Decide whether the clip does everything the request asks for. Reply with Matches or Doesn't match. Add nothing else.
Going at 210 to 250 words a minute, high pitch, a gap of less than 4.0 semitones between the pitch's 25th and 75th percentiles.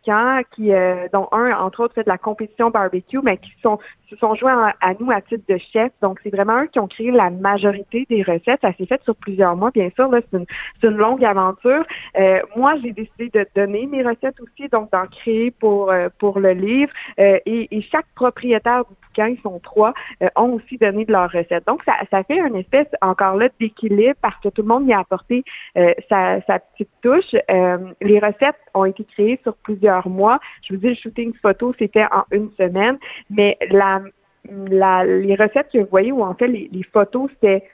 Matches